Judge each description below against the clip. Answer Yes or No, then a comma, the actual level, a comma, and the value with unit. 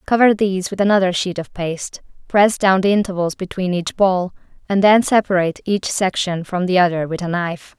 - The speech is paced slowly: No, average, 195 wpm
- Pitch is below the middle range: No, medium, 185 Hz